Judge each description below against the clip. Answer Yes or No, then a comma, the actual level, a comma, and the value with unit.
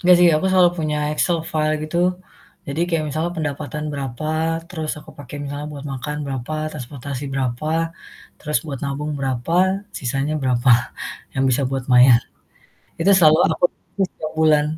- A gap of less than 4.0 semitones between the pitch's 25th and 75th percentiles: Yes, narrow, 2.6 semitones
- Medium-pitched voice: Yes, medium, 150 Hz